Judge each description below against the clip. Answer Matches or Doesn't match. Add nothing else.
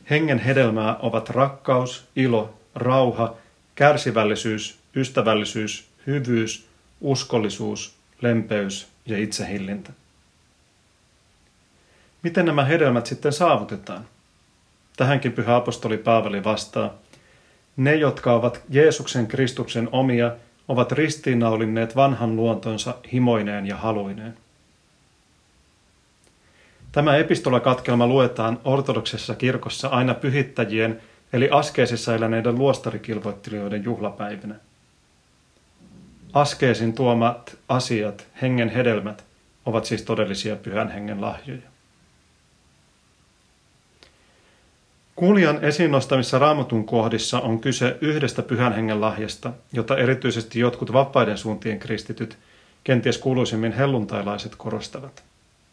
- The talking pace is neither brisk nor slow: Doesn't match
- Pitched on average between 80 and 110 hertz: Doesn't match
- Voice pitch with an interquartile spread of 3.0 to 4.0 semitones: Matches